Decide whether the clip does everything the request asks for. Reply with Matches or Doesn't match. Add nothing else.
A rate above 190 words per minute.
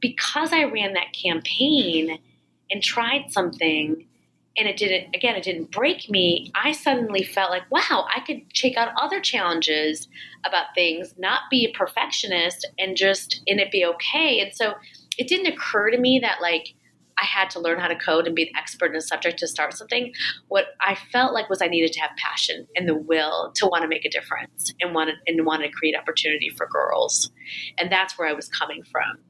Matches